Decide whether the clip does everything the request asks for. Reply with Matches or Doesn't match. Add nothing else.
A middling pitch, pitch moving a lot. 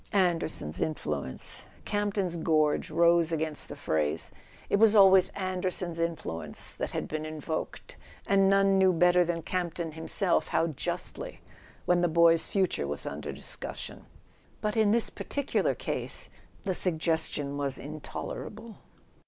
Doesn't match